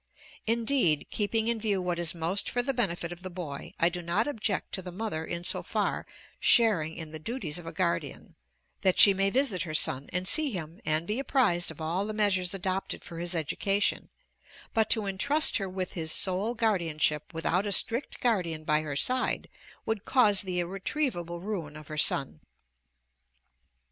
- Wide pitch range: No, average, 4.7 semitones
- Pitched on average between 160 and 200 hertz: Yes, medium, 185 Hz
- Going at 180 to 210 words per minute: Yes, average, 185 wpm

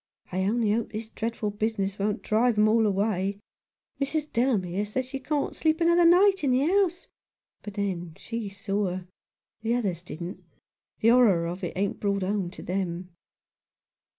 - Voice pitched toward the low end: No, high, 210 Hz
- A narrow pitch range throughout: No, average, 4.4 semitones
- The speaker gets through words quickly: No, average, 165 wpm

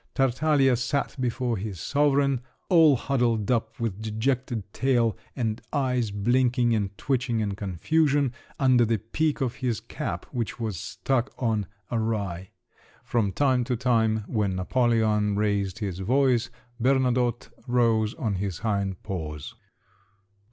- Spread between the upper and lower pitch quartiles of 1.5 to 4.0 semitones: Yes, average, 3.6 semitones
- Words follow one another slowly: Yes, slow, 130 wpm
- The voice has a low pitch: Yes, low, 115 Hz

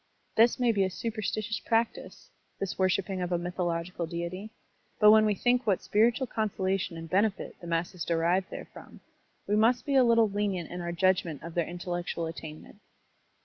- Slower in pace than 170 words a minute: No, average, 180 wpm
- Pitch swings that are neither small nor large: Yes, average, 3.9 semitones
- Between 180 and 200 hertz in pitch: Yes, high, 190 Hz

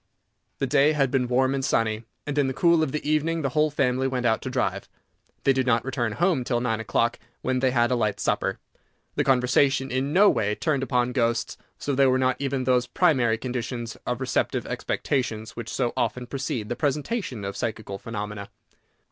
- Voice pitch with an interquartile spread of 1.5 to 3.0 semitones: Yes, average, 2.7 semitones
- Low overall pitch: Yes, low, 130 Hz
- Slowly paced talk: No, average, 200 wpm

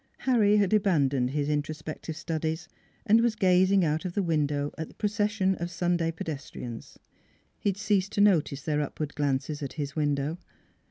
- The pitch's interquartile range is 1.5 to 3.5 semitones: No, average, 4.9 semitones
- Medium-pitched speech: Yes, medium, 160 Hz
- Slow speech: No, average, 165 wpm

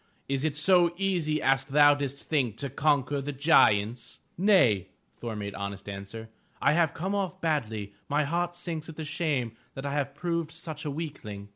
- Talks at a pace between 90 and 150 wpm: No, average, 175 wpm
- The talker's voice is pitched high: No, medium, 145 Hz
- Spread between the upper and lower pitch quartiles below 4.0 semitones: No, average, 5.3 semitones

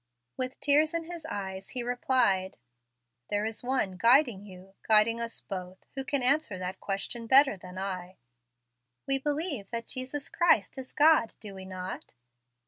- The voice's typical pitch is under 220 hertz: No, high, 230 Hz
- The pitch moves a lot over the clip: Yes, wide, 5.9 semitones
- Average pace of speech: Yes, average, 155 wpm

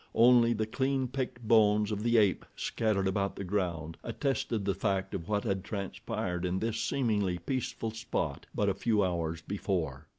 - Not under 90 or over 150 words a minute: No, average, 170 wpm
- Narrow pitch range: No, average, 3.4 semitones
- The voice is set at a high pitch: No, low, 105 Hz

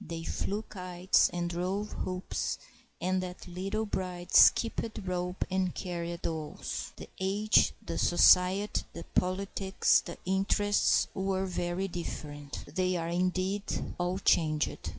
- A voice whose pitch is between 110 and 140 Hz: No, medium, 185 Hz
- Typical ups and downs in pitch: No, narrow, 1.8 semitones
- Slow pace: Yes, slow, 125 wpm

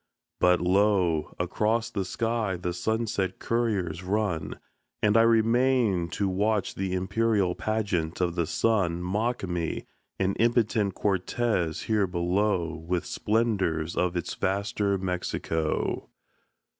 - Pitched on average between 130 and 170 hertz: No, very low, 95 Hz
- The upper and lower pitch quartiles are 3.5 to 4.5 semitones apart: Yes, average, 3.8 semitones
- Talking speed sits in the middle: No, slow, 120 wpm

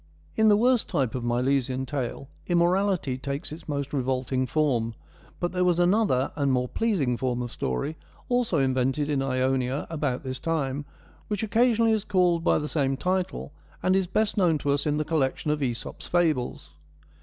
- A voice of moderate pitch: Yes, medium, 145 Hz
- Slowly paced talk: No, average, 175 wpm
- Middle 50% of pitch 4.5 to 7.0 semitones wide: Yes, wide, 5.6 semitones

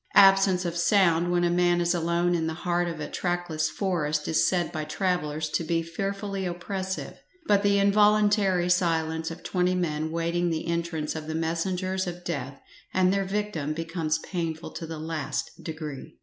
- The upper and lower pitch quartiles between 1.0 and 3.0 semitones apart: Yes, narrow, 2.5 semitones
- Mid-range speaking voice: Yes, medium, 175 Hz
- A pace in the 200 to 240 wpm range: No, average, 175 wpm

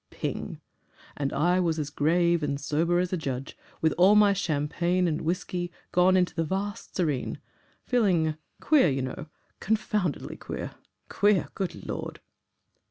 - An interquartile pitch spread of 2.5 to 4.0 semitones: Yes, average, 3.7 semitones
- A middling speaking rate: Yes, average, 145 wpm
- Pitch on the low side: No, medium, 175 Hz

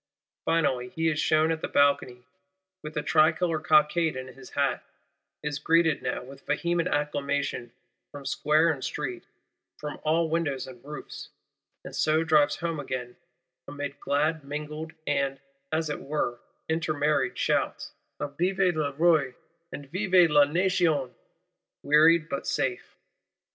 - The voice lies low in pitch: No, medium, 150 Hz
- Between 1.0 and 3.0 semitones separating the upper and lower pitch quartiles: Yes, narrow, 2.4 semitones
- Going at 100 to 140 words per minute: Yes, slow, 135 wpm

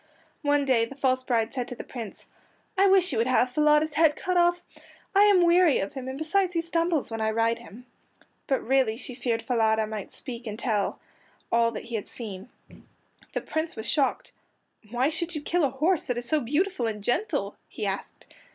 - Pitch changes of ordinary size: No, wide, 5.8 semitones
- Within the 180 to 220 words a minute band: Yes, average, 200 wpm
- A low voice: No, very high, 260 Hz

